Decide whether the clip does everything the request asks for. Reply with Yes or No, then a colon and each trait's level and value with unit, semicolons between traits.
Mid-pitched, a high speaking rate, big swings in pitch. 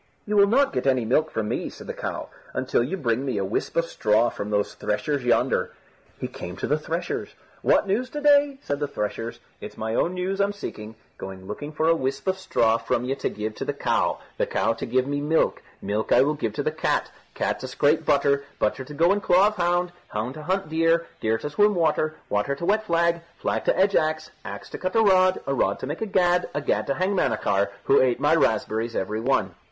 Yes: medium, 150 Hz; fast, 235 wpm; wide, 7.4 semitones